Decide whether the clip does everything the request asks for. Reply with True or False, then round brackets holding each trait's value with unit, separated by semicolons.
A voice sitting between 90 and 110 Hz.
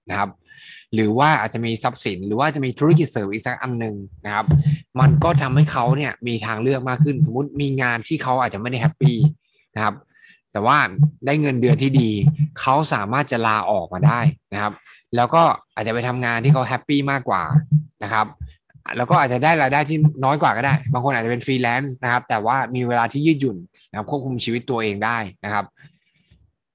False (130 Hz)